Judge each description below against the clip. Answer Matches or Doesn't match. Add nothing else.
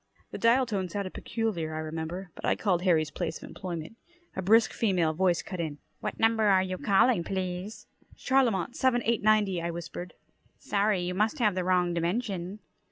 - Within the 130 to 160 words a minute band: Doesn't match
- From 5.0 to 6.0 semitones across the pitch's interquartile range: Doesn't match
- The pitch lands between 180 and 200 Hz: Matches